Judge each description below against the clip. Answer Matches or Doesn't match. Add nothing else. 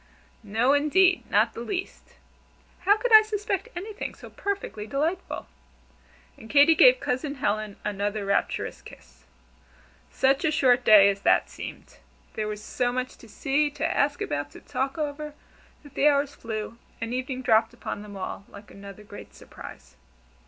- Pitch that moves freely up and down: Matches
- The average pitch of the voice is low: Doesn't match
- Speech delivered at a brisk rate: Doesn't match